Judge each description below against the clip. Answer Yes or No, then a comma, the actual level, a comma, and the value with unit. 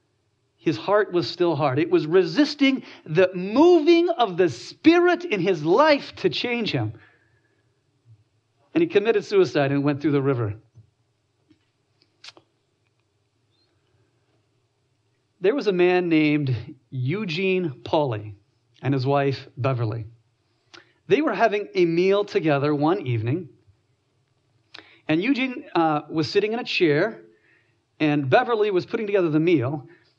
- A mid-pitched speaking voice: Yes, medium, 145 Hz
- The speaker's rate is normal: No, slow, 125 wpm